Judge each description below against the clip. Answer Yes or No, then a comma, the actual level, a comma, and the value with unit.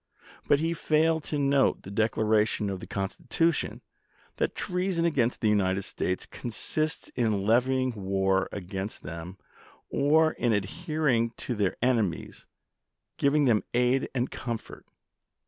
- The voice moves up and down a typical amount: No, wide, 6.3 semitones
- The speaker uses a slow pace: Yes, slow, 130 wpm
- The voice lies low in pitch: Yes, low, 120 Hz